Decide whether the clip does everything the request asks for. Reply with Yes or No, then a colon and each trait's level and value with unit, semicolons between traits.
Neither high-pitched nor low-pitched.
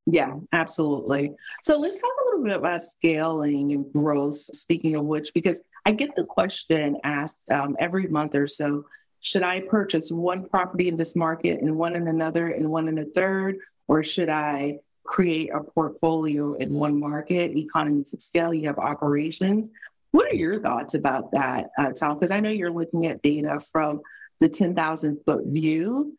Yes: medium, 160 Hz